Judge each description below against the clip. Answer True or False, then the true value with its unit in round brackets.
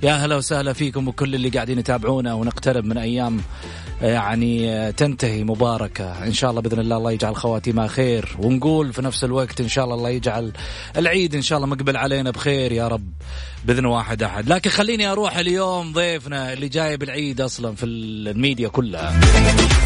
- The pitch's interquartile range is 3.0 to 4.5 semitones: True (3.6 semitones)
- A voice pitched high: False (125 Hz)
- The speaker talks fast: True (170 wpm)